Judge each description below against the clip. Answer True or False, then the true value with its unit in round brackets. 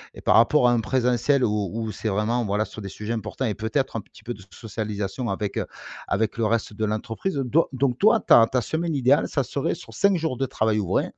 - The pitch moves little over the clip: False (3.7 semitones)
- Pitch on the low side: True (115 Hz)